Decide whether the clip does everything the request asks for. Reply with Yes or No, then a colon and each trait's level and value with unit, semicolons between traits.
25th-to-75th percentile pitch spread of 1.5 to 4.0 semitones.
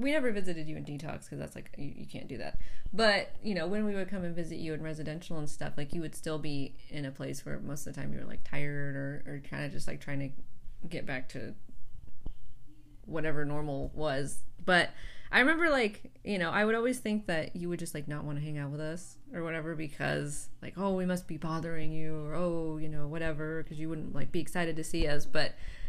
Yes: average, 3.0 semitones